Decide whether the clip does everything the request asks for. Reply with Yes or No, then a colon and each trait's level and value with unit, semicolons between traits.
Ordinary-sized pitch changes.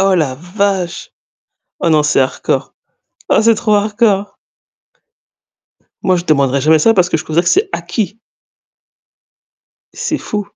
Yes: average, 4.7 semitones